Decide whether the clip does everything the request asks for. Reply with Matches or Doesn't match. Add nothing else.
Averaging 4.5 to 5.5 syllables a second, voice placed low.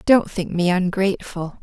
Doesn't match